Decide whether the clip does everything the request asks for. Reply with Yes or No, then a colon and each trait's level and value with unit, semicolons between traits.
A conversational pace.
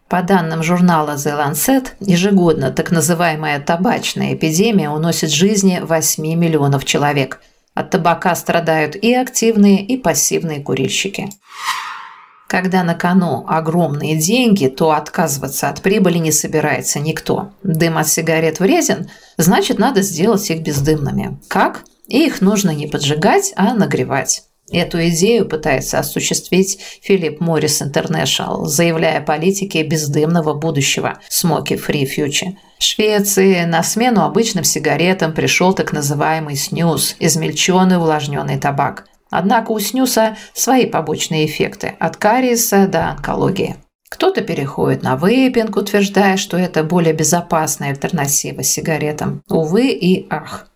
Yes: average, 125 wpm